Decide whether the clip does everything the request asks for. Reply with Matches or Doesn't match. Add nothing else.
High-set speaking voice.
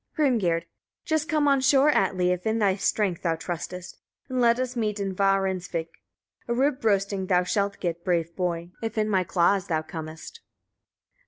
Matches